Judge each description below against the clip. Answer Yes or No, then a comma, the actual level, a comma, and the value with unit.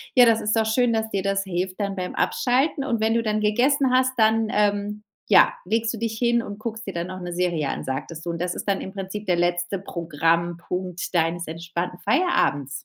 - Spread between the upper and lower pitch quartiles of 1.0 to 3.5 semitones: No, average, 4.3 semitones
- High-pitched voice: Yes, high, 200 Hz